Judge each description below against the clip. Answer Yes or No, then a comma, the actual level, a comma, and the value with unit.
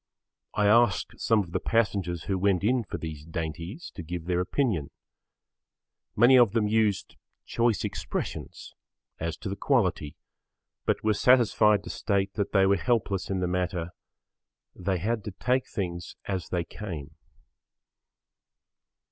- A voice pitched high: No, low, 100 Hz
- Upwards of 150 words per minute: No, average, 145 wpm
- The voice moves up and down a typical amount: Yes, average, 4.1 semitones